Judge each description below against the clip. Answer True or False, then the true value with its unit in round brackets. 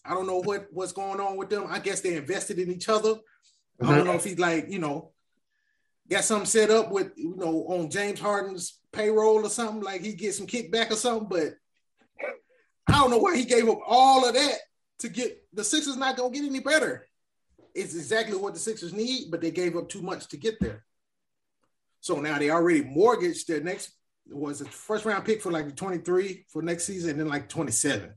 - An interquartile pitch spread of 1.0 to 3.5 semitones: False (4.8 semitones)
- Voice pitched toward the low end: False (200 Hz)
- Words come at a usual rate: False (225 wpm)